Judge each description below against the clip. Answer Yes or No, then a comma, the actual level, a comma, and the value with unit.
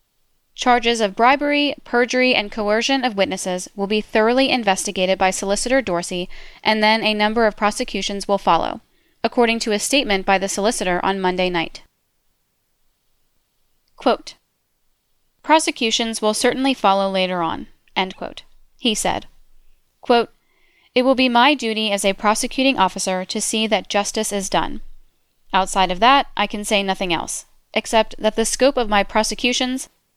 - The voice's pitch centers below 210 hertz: No, high, 215 Hz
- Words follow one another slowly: No, average, 150 wpm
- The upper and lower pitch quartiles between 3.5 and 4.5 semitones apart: Yes, average, 4.1 semitones